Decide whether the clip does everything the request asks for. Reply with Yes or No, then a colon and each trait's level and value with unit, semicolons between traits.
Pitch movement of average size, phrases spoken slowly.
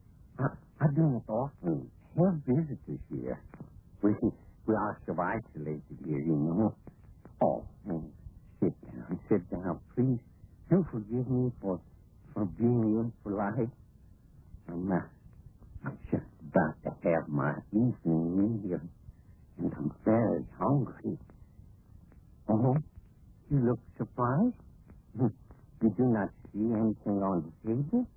Yes: average, 4.9 semitones; slow, 120 wpm